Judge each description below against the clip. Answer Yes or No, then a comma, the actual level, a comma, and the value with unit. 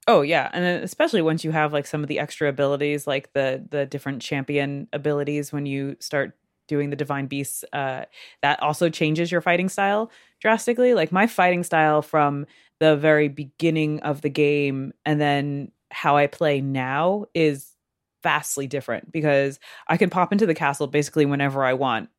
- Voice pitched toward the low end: No, medium, 150 Hz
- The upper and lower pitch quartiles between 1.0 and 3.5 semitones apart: Yes, narrow, 2.4 semitones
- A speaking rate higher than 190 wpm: No, average, 175 wpm